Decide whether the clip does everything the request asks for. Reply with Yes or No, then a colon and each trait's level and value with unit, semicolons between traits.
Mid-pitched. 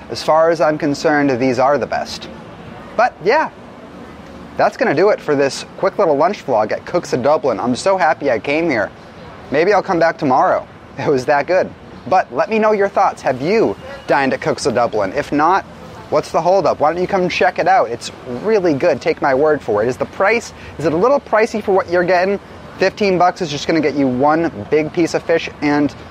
Yes: medium, 165 Hz